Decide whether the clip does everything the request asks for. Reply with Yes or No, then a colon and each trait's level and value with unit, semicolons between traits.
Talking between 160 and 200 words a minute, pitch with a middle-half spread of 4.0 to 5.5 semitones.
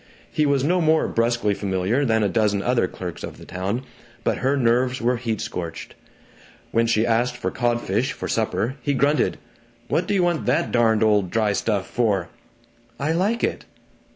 Yes: average, 175 wpm; average, 4.6 semitones